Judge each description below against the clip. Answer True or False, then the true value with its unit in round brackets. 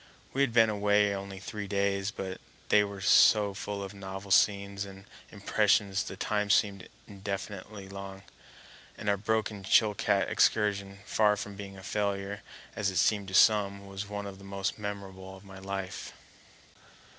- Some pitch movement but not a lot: False (1.0 semitones)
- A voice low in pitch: True (100 Hz)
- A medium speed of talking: True (160 wpm)